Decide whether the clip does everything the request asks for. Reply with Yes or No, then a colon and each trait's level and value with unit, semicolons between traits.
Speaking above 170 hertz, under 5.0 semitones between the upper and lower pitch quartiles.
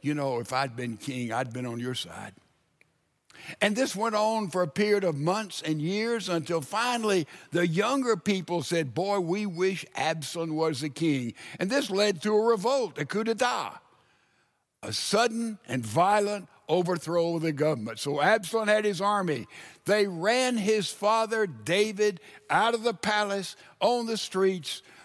No: high, 190 Hz; wide, 5.4 semitones